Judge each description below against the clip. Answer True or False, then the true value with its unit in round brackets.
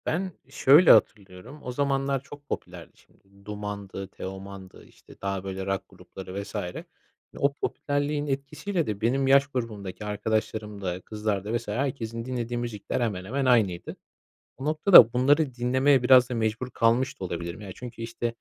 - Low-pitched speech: True (115 Hz)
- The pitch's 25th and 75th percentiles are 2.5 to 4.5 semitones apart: False (5.2 semitones)